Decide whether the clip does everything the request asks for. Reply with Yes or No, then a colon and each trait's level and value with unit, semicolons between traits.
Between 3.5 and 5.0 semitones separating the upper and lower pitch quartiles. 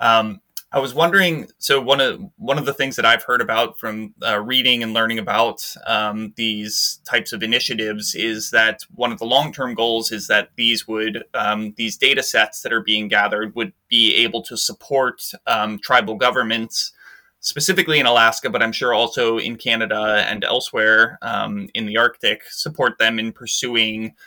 No: average, 3.0 semitones